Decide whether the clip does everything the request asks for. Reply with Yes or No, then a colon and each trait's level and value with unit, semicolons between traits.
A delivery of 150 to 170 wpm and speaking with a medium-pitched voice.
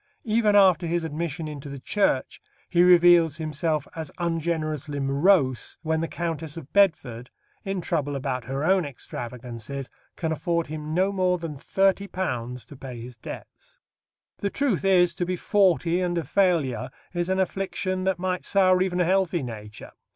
Yes: average, 160 wpm; medium, 165 Hz